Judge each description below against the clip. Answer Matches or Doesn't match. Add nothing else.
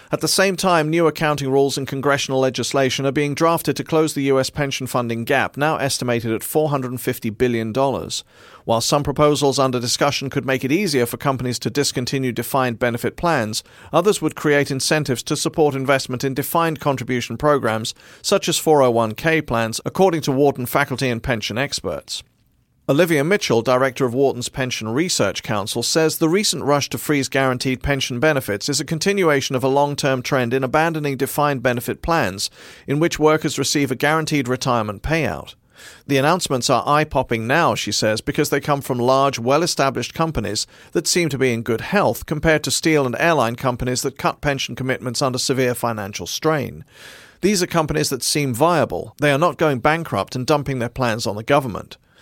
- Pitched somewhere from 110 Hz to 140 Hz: Matches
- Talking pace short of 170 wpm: Doesn't match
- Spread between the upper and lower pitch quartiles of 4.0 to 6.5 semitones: Doesn't match